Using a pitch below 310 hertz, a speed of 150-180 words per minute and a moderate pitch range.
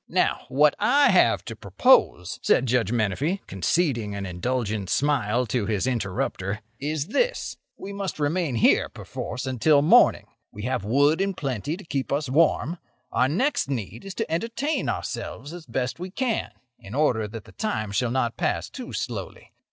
No: low, 135 Hz; average, 165 wpm; wide, 7.1 semitones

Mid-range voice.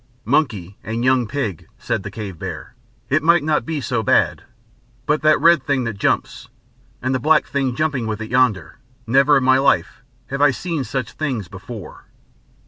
No: low, 130 Hz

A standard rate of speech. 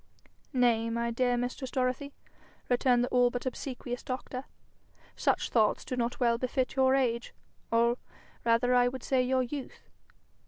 Yes: average, 150 wpm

